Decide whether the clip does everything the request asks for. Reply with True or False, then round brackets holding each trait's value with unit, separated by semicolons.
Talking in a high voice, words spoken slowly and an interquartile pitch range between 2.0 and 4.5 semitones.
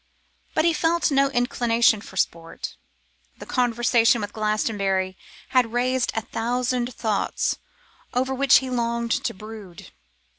True (235 Hz; 125 wpm; 2.9 semitones)